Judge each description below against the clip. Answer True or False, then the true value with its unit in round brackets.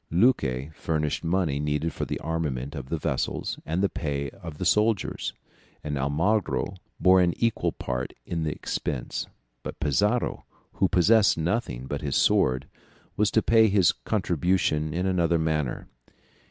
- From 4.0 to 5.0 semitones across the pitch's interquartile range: True (4.7 semitones)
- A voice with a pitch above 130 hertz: False (80 Hz)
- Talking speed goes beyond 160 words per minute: False (150 wpm)